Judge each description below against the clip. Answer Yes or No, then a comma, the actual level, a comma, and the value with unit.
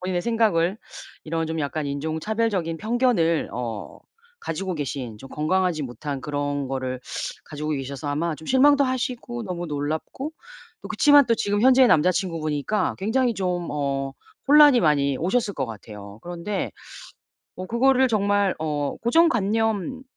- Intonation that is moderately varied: No, wide, 7.7 semitones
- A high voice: No, medium, 175 Hz